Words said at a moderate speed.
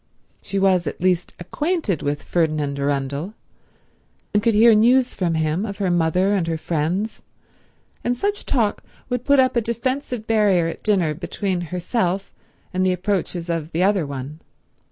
Yes: average, 160 wpm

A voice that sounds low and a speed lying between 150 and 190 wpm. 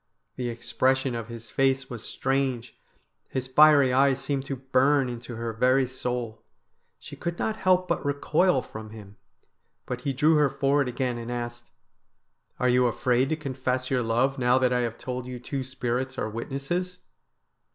Yes: low, 130 Hz; average, 170 wpm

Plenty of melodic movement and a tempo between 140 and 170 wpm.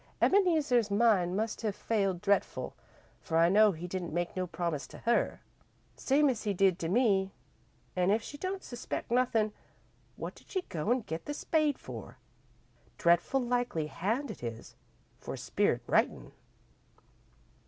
Yes: wide, 5.7 semitones; average, 155 wpm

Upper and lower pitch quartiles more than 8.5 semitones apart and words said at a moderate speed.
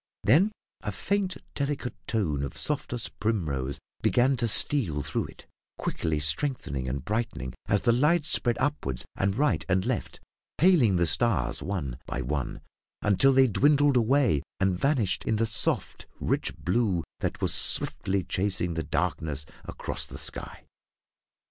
Yes: wide, 9.0 semitones; average, 145 wpm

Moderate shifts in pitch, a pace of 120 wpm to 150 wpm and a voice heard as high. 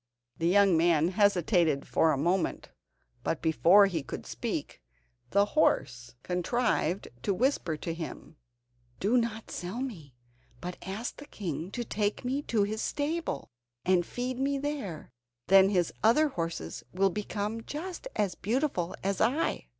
No: wide, 5.9 semitones; average, 145 wpm; high, 195 Hz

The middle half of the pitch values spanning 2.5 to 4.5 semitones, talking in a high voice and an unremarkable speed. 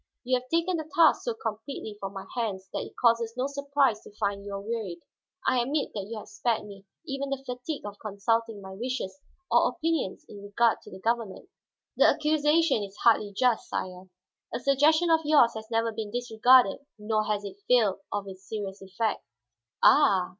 No: average, 5.2 semitones; high, 230 Hz; average, 190 wpm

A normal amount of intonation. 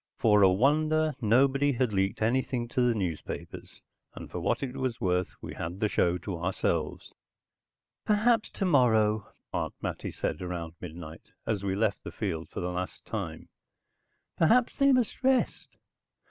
No: wide, 7.2 semitones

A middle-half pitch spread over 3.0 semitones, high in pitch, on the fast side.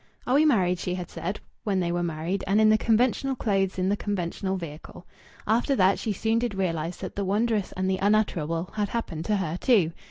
Yes: average, 3.5 semitones; high, 195 Hz; fast, 215 wpm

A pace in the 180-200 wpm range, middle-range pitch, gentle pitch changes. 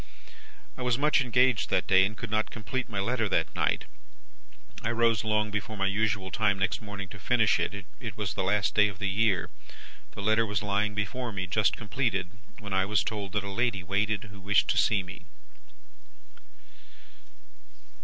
No: average, 185 wpm; low, 105 Hz; narrow, 2.3 semitones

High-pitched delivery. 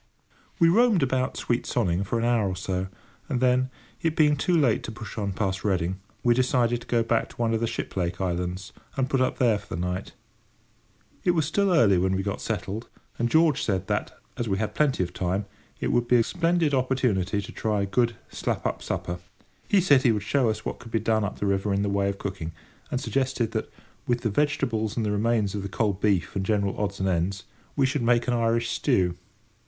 No: low, 110 Hz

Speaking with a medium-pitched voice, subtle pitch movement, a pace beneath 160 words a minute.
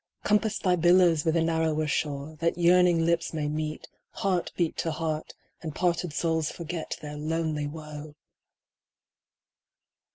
Yes: medium, 160 Hz; narrow, 2.1 semitones; slow, 135 wpm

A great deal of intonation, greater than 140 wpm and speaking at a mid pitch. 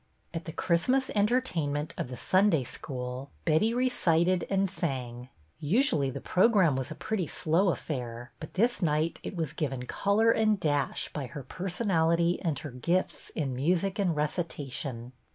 Yes: wide, 5.8 semitones; average, 155 wpm; medium, 165 Hz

